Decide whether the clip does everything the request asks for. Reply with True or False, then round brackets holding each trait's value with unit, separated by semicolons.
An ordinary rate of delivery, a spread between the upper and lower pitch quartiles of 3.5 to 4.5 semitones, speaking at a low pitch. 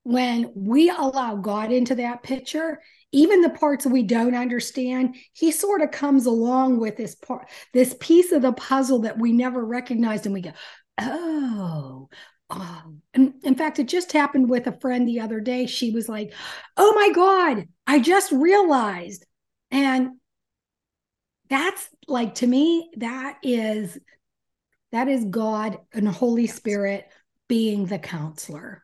False (150 wpm; 4.1 semitones; 250 Hz)